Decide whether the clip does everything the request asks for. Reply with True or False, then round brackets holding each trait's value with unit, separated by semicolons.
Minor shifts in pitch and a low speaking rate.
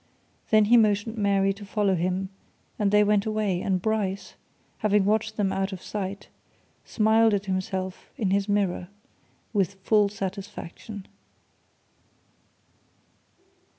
True (1.7 semitones; 120 wpm)